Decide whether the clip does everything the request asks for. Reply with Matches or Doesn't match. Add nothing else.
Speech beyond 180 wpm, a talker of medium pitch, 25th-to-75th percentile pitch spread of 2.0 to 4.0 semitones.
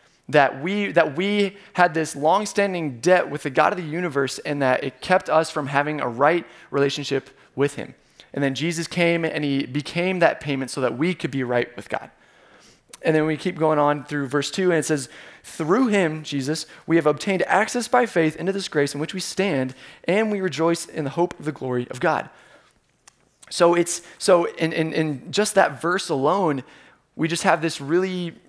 Matches